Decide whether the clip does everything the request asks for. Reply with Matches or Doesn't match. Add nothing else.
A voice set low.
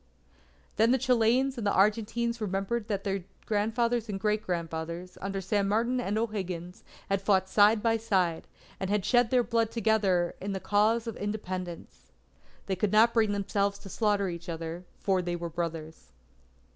Doesn't match